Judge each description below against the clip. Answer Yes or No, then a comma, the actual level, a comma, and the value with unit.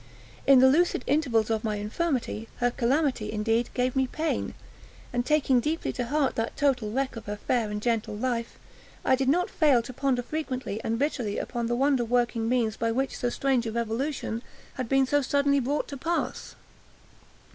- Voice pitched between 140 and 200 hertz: No, very high, 250 Hz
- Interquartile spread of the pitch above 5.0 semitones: No, average, 3.2 semitones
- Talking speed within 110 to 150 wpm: No, average, 185 wpm